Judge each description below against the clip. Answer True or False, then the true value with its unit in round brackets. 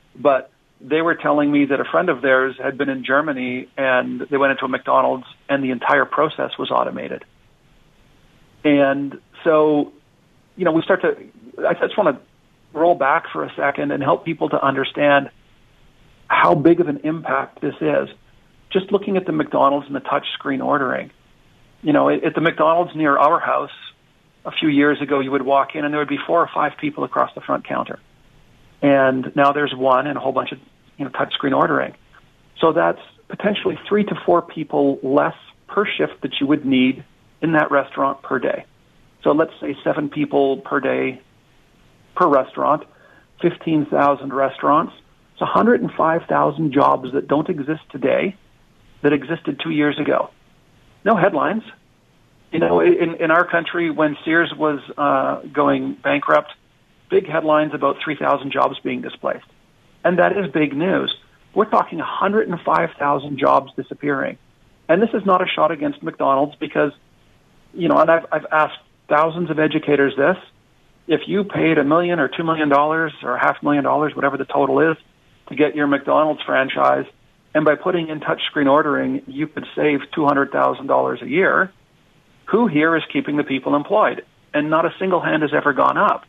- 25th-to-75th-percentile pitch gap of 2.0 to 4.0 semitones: True (3.0 semitones)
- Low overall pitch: False (150 Hz)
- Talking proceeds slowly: False (175 wpm)